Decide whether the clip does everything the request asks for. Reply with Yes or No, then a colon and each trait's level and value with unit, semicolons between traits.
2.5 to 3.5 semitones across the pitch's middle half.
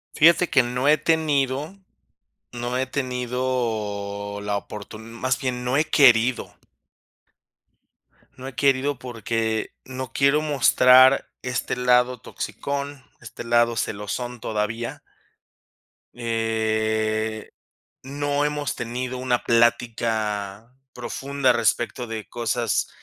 Yes: average, 2.8 semitones